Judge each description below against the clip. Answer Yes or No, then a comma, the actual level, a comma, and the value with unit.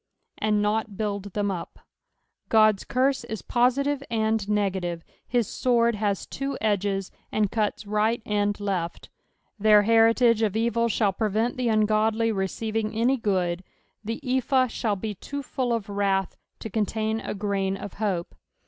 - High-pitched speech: Yes, high, 215 Hz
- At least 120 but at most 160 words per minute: Yes, average, 150 wpm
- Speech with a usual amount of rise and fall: No, narrow, 2.2 semitones